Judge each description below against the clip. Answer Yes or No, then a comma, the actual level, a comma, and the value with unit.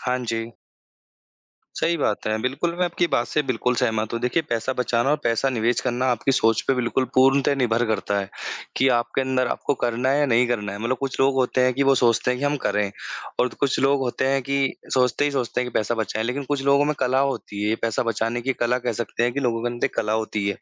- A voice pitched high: No, low, 125 Hz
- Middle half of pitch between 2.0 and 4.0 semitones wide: Yes, average, 2.8 semitones